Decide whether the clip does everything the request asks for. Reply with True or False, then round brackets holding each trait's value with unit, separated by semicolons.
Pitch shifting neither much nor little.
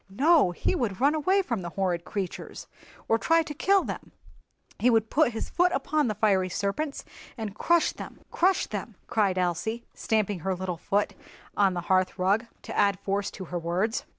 False (6.8 semitones)